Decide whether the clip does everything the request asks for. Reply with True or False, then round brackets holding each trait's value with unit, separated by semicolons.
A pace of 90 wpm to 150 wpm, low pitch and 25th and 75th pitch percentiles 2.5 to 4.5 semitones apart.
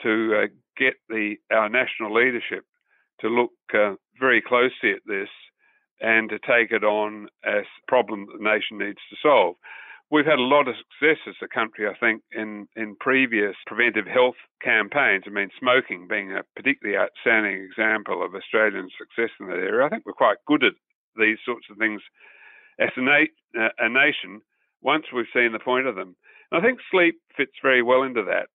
False (185 wpm; 120 Hz; 3.7 semitones)